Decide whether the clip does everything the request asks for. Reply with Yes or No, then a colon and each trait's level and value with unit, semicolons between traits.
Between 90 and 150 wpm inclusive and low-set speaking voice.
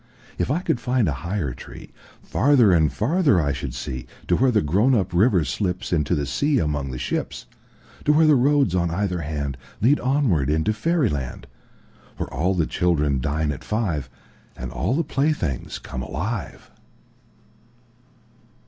Yes: average, 140 wpm; very low, 90 Hz